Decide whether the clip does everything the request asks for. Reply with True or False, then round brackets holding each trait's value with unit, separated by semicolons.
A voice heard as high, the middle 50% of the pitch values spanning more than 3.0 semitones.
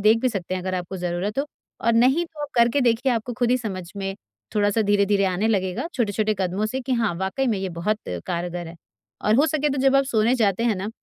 True (215 Hz; 4.6 semitones)